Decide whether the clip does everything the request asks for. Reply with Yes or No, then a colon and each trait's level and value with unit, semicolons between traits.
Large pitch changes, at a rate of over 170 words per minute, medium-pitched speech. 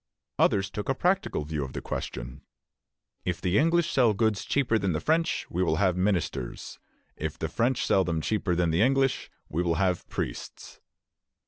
No: wide, 6.3 semitones; average, 180 wpm; very low, 95 Hz